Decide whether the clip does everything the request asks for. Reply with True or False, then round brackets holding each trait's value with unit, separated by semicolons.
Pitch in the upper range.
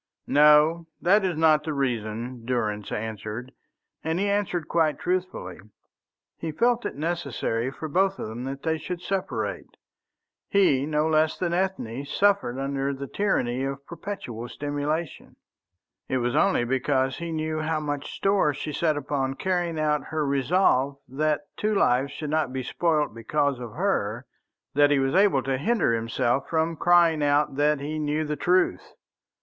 False (150 Hz)